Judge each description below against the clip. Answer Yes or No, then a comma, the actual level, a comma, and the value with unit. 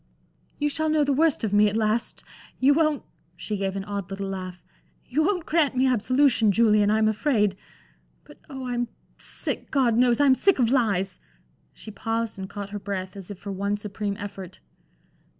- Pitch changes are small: No, average, 4.8 semitones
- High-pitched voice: Yes, high, 215 Hz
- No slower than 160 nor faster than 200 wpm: Yes, average, 185 wpm